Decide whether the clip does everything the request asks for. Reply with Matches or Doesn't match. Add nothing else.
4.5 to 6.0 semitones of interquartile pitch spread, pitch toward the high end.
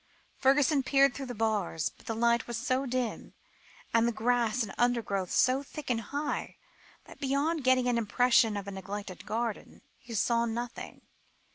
Doesn't match